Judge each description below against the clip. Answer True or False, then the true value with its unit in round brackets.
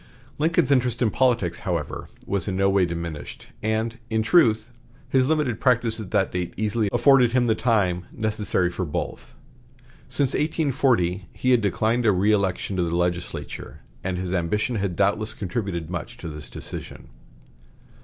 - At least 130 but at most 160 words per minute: True (155 wpm)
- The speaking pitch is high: False (105 Hz)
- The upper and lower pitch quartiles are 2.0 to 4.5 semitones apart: False (5.1 semitones)